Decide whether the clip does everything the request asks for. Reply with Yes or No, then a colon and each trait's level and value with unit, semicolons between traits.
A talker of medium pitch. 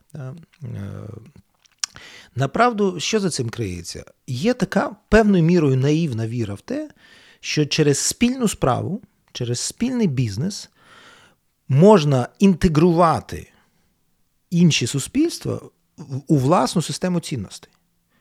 Yes: medium, 165 Hz